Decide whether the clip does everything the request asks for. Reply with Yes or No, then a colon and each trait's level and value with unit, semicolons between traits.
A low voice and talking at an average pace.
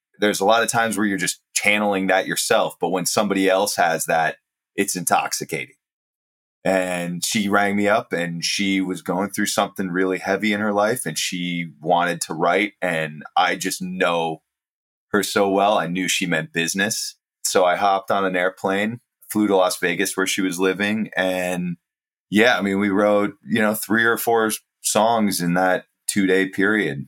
Yes: very low, 95 Hz; average, 185 wpm